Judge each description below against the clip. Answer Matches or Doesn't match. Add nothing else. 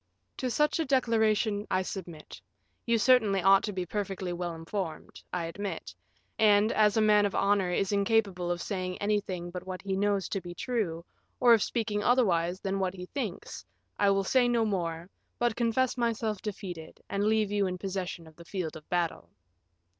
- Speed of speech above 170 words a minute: Matches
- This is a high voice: Matches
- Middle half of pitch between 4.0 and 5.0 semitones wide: Doesn't match